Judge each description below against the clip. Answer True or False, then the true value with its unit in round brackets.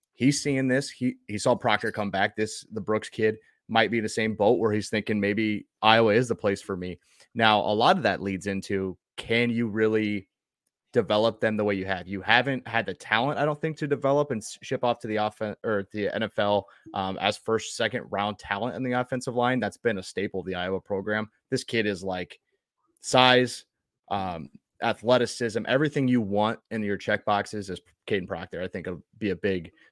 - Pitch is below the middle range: True (110 Hz)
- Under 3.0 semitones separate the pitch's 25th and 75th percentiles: False (3.4 semitones)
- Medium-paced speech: False (215 wpm)